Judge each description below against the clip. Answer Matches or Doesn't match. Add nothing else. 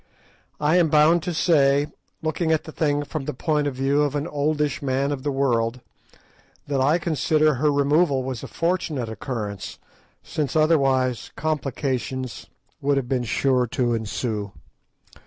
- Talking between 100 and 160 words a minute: Matches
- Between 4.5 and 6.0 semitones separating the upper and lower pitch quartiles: Doesn't match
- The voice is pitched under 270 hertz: Matches